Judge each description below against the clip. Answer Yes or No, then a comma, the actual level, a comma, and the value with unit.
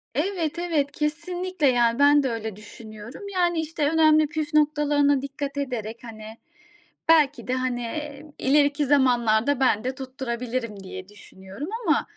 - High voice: Yes, very high, 275 Hz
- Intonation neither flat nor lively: Yes, average, 4.3 semitones